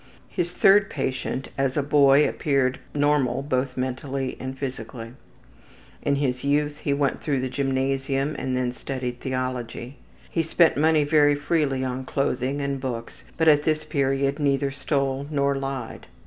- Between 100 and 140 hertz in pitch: Yes, low, 135 Hz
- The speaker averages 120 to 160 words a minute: Yes, average, 150 wpm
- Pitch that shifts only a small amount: Yes, narrow, 1.9 semitones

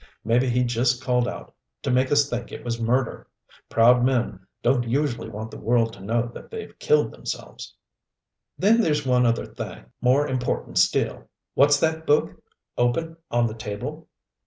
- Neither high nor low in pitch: No, low, 125 Hz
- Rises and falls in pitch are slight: No, average, 3.4 semitones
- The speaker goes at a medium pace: Yes, average, 165 wpm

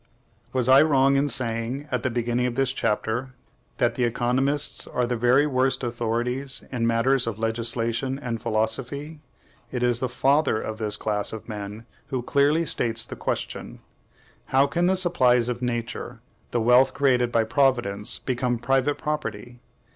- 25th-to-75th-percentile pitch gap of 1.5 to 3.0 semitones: Yes, average, 2.7 semitones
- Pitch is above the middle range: No, low, 125 Hz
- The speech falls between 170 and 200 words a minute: No, average, 160 wpm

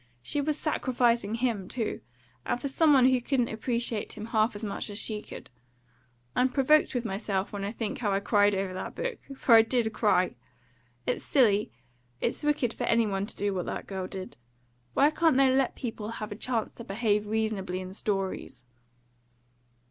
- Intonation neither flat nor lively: Yes, average, 3.9 semitones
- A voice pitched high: Yes, high, 225 Hz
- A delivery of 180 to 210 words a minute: Yes, average, 185 wpm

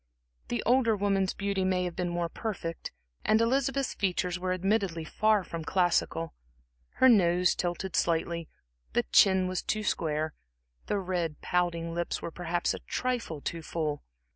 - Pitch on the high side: No, medium, 180 Hz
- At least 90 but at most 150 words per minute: Yes, average, 145 wpm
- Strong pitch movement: No, average, 3.1 semitones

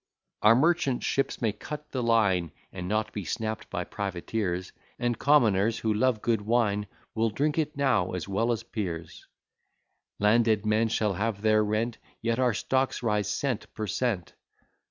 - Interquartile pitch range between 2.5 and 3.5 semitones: Yes, average, 2.9 semitones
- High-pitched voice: No, low, 110 Hz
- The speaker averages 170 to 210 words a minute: No, average, 160 wpm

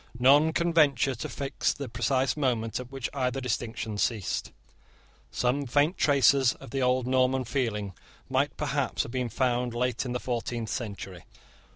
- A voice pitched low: Yes, low, 125 Hz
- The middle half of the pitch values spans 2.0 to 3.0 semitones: Yes, narrow, 2.6 semitones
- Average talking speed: Yes, average, 160 wpm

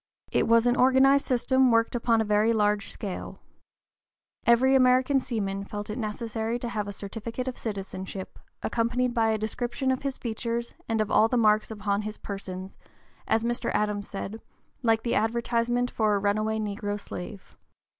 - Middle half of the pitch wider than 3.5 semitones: No, narrow, 2.5 semitones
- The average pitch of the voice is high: Yes, high, 225 Hz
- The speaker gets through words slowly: No, average, 165 wpm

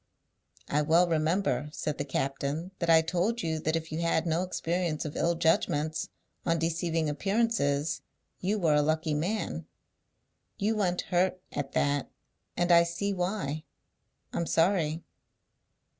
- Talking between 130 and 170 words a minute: Yes, average, 145 wpm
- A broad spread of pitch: No, average, 2.7 semitones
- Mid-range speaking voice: Yes, medium, 165 Hz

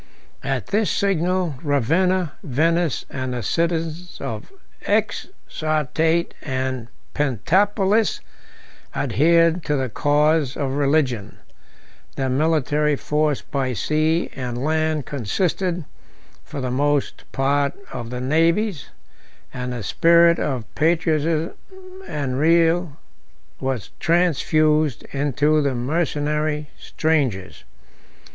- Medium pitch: Yes, medium, 150 Hz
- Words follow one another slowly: Yes, slow, 100 wpm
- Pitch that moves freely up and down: No, average, 3.7 semitones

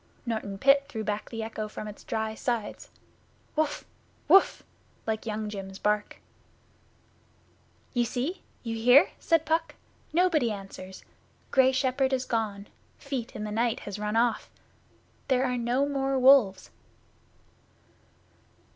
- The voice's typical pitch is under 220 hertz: No, high, 235 Hz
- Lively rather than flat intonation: No, average, 4.0 semitones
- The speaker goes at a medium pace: No, slow, 130 wpm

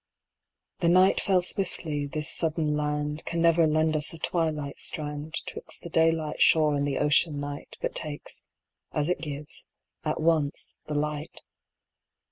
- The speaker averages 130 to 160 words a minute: Yes, average, 150 wpm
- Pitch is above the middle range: No, medium, 155 Hz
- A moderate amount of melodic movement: No, narrow, 1.8 semitones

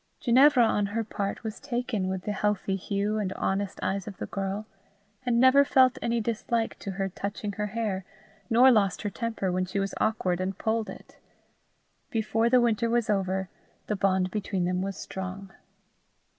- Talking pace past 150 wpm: Yes, average, 175 wpm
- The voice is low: No, high, 205 Hz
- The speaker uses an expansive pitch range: No, average, 3.2 semitones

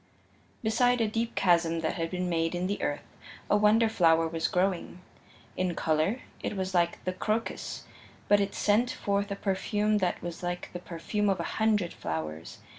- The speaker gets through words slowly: No, average, 180 wpm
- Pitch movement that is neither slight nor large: Yes, average, 3.7 semitones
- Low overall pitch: No, medium, 185 Hz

